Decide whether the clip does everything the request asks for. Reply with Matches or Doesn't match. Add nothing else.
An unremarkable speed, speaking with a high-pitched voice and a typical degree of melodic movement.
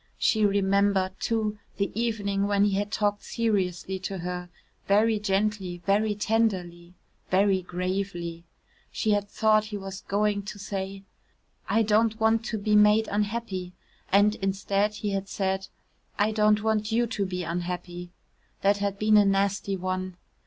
Doesn't match